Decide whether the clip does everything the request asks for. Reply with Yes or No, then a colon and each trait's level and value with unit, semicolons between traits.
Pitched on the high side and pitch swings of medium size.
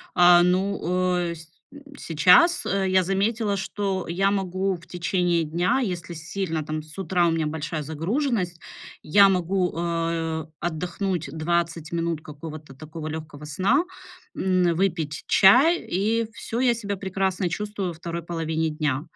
No: medium, 175 Hz; average, 3.3 semitones